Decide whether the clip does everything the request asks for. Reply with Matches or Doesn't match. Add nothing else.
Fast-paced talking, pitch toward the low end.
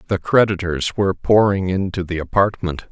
Doesn't match